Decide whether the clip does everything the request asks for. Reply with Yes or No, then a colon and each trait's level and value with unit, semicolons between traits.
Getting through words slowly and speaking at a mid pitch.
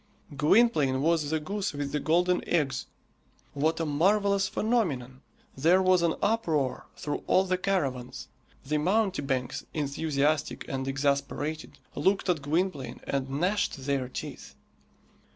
Yes: slow, 125 wpm; medium, 155 Hz